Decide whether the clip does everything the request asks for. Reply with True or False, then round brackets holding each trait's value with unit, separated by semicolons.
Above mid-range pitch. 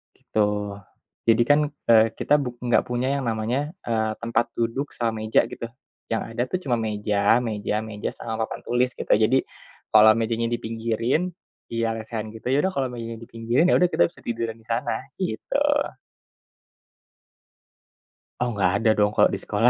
False (115 Hz)